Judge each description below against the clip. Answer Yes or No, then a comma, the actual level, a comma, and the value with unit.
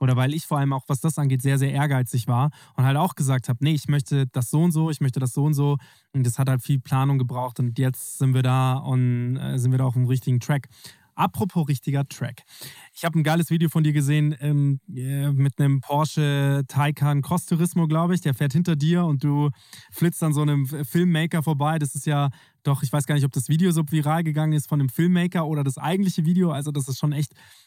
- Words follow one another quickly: Yes, fast, 235 wpm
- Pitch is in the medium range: Yes, medium, 145 Hz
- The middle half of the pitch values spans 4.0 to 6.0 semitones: No, average, 2.8 semitones